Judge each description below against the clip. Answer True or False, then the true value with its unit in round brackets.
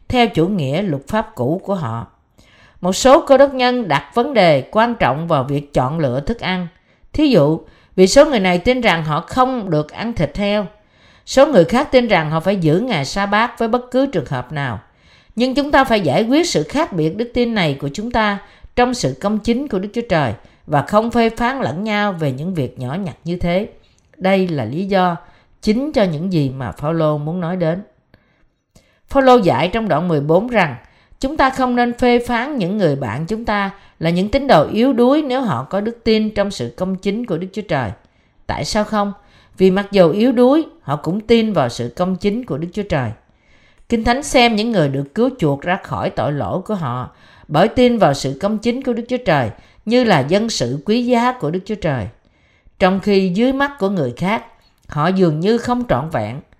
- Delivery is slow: False (220 wpm)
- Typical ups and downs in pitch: False (7.1 semitones)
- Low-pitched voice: False (195 Hz)